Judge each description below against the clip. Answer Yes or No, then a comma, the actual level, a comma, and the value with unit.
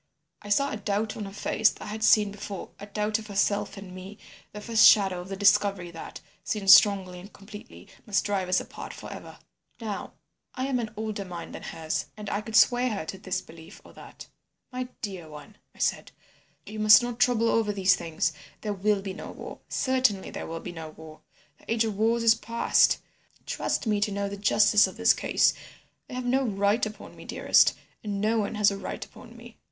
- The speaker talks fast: Yes, fast, 215 wpm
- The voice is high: Yes, high, 205 Hz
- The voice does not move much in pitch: Yes, narrow, 2.2 semitones